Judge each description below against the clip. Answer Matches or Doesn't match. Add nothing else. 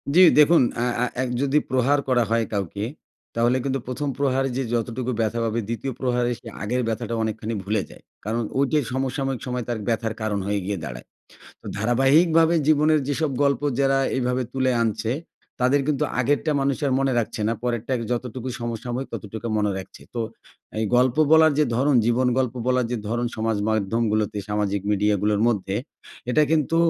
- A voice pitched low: Matches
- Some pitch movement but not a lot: Matches